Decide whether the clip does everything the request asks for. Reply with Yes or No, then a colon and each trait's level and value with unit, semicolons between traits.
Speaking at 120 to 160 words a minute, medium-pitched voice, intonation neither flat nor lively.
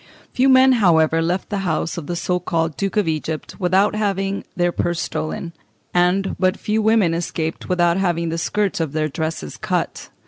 No: average, 180 wpm; medium, 175 Hz; average, 3.2 semitones